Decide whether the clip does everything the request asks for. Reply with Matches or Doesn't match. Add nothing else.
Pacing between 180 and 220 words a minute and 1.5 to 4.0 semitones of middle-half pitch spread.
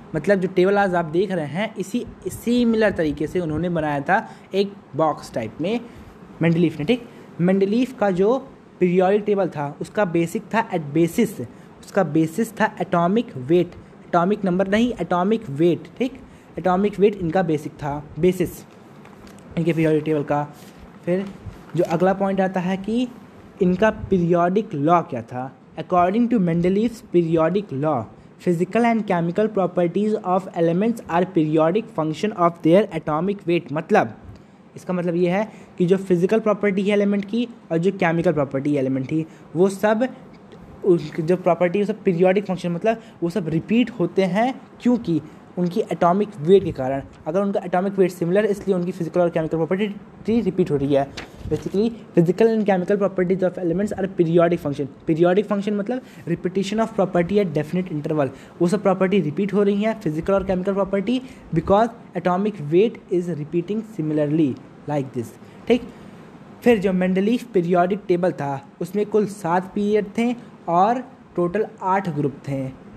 Doesn't match